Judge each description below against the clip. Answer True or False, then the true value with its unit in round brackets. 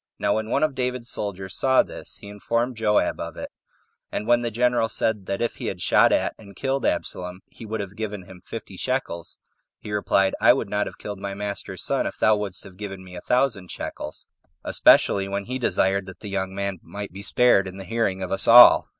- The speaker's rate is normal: False (220 wpm)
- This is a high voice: False (100 Hz)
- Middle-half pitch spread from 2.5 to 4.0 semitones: True (3.2 semitones)